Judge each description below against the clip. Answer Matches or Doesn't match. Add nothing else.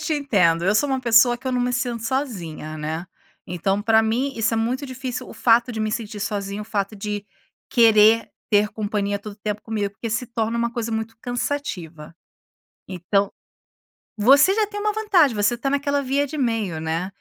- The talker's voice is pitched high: Matches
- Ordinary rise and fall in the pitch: Matches